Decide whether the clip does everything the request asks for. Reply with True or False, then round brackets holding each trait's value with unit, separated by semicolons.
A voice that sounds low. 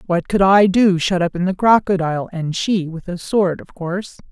False (185 Hz)